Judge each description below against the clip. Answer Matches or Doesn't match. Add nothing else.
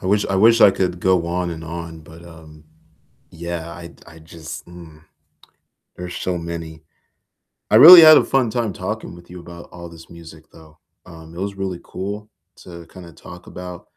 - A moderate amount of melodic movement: Doesn't match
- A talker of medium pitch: Doesn't match